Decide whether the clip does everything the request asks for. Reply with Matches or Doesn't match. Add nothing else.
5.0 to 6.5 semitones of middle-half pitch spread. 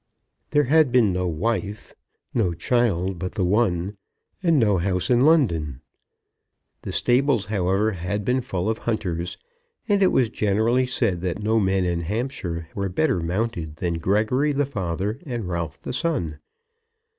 Matches